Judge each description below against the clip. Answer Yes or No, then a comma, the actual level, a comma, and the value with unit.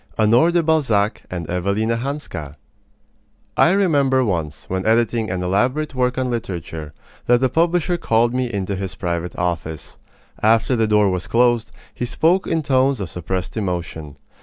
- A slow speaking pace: No, average, 155 wpm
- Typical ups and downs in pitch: No, wide, 6.2 semitones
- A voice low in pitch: Yes, low, 110 Hz